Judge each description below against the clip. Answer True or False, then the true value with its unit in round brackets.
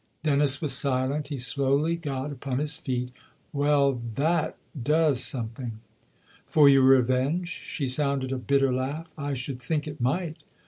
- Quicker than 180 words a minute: False (170 wpm)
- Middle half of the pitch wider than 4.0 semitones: False (2.4 semitones)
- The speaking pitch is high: False (140 Hz)